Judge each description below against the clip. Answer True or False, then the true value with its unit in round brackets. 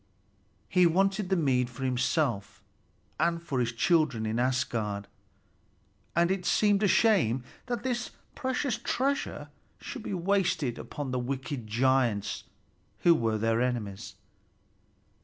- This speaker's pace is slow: True (125 wpm)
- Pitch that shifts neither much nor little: False (8.0 semitones)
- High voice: False (140 Hz)